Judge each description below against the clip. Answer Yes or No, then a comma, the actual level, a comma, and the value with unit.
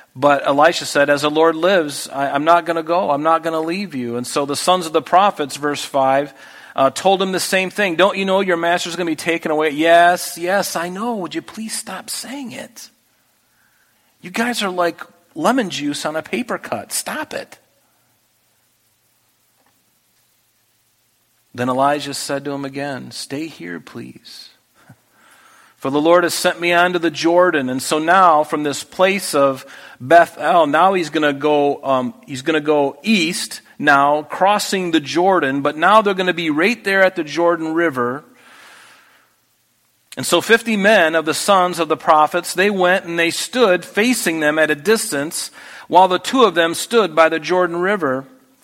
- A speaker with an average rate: Yes, average, 180 wpm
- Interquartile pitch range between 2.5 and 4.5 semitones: Yes, average, 4.1 semitones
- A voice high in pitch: No, medium, 170 Hz